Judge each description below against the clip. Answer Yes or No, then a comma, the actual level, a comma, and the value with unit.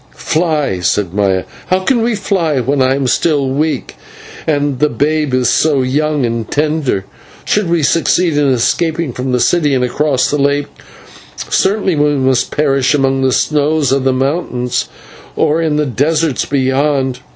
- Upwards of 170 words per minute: No, average, 160 wpm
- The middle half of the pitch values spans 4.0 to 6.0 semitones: No, average, 3.2 semitones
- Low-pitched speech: No, medium, 145 Hz